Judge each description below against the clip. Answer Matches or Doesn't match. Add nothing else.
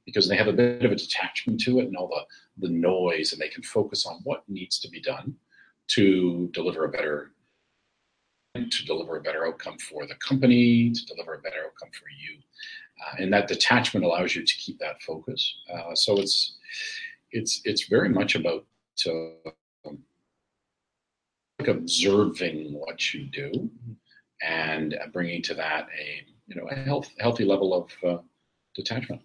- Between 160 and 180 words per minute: Matches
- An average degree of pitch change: Doesn't match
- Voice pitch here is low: Matches